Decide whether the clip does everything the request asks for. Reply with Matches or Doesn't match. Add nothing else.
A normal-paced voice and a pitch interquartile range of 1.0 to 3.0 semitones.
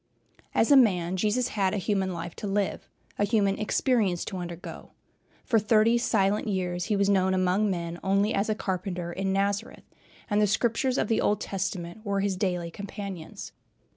Matches